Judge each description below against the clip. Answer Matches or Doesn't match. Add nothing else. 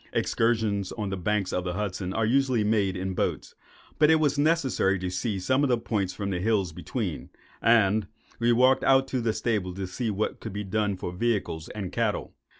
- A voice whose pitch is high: Doesn't match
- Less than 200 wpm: Doesn't match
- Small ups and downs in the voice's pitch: Doesn't match